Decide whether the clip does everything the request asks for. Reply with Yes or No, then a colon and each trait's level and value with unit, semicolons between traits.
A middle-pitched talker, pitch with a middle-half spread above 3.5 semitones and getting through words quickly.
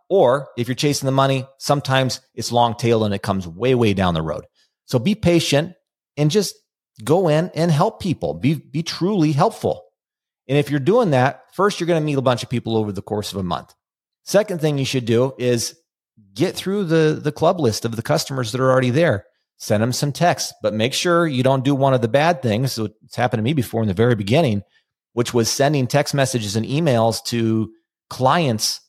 No: low, 130 Hz; average, 4.8 semitones; fast, 220 wpm